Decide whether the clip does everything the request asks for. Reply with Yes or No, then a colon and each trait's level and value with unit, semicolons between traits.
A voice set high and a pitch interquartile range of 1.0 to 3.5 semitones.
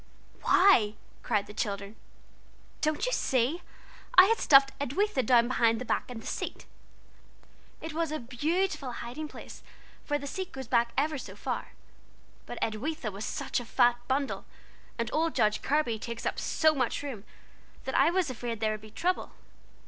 No: very high, 265 Hz; average, 5.1 semitones